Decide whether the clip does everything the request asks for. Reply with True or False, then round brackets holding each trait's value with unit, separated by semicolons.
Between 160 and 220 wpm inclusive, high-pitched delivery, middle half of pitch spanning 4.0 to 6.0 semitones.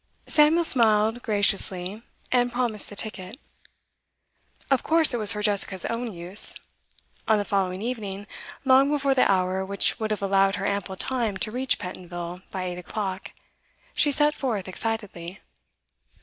False (150 wpm; 210 Hz; 4.3 semitones)